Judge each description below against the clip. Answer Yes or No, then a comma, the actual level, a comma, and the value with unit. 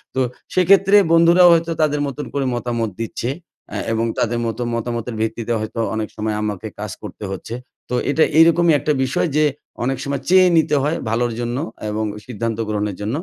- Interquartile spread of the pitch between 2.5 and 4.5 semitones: No, wide, 5.6 semitones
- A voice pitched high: No, low, 120 Hz